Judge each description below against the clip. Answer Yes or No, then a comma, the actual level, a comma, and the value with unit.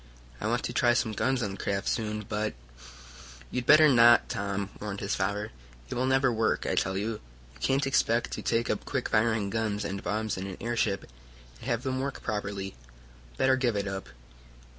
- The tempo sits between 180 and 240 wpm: Yes, average, 200 wpm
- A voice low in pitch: Yes, low, 110 Hz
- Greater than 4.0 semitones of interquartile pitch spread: No, average, 3.3 semitones